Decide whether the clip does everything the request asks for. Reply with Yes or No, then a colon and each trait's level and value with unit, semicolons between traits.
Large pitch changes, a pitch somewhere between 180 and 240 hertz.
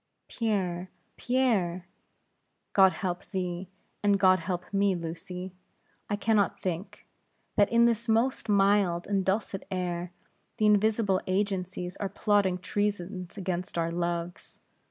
No: narrow, 2.5 semitones; high, 190 Hz